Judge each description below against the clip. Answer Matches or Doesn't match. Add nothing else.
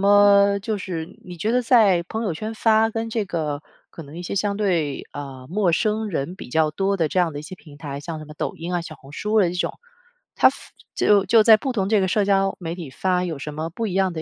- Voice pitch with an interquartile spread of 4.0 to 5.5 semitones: Matches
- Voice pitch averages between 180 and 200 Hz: Matches